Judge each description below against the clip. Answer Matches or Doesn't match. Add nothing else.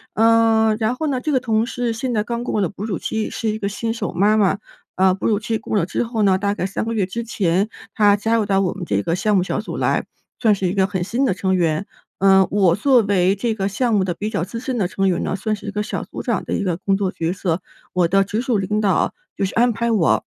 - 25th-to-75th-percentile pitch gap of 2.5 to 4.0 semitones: Matches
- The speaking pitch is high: Matches